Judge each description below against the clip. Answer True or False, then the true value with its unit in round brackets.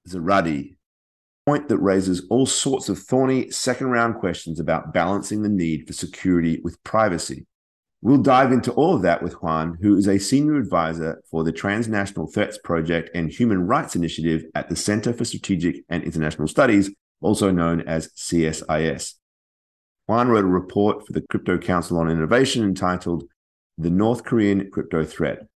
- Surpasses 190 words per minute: False (165 wpm)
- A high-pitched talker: False (90 Hz)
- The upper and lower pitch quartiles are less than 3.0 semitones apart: False (4.4 semitones)